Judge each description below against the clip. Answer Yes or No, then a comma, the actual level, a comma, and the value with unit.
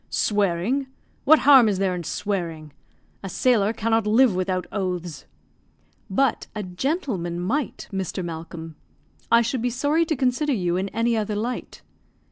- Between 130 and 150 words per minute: Yes, average, 145 wpm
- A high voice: Yes, high, 210 Hz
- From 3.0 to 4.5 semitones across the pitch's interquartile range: No, wide, 5.6 semitones